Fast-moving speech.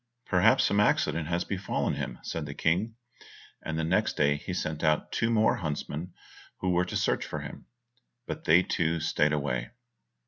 No: average, 175 wpm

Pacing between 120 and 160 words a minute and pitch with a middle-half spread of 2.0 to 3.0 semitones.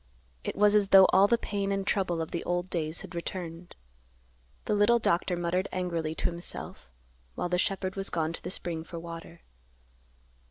No: average, 185 wpm; narrow, 2.5 semitones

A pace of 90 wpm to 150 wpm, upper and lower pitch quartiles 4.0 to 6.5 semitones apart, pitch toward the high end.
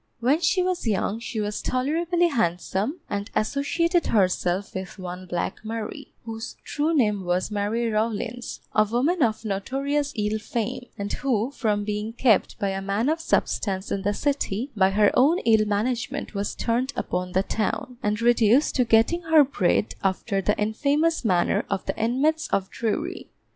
No: average, 165 wpm; average, 5.2 semitones; high, 225 Hz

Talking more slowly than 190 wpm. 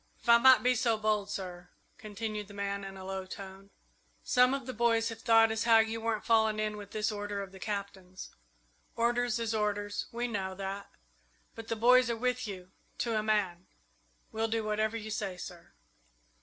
No: average, 195 wpm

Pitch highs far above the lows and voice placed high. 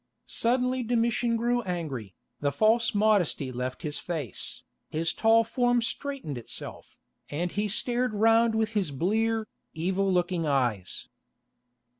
Yes: wide, 6.7 semitones; high, 210 Hz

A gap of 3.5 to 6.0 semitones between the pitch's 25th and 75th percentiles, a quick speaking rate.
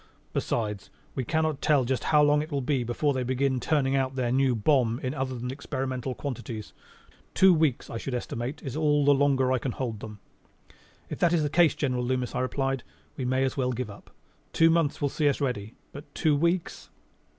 No: average, 2.8 semitones; fast, 210 wpm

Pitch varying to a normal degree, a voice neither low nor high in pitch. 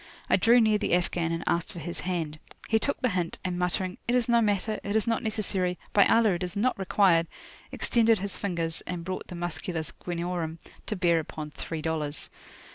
Yes: average, 4.1 semitones; medium, 180 Hz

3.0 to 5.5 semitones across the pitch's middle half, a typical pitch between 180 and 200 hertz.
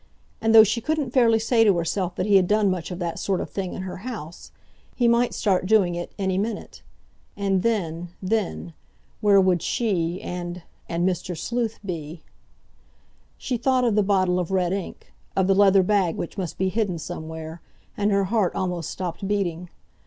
Yes: average, 3.3 semitones; high, 190 Hz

